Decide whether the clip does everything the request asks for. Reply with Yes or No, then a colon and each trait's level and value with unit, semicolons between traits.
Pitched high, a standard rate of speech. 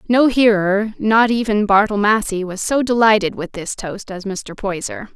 Yes: high, 210 Hz; average, 175 wpm